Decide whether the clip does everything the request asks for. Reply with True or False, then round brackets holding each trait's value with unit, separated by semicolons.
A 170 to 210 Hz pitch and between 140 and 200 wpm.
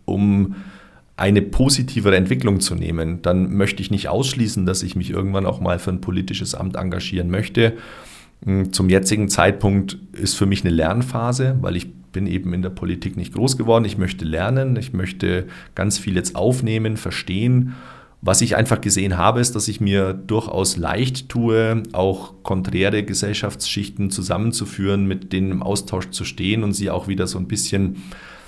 False (100 Hz; 170 wpm)